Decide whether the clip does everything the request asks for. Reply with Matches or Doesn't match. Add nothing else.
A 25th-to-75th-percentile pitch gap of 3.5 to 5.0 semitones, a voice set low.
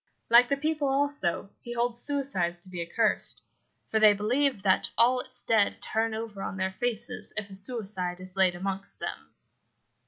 Doesn't match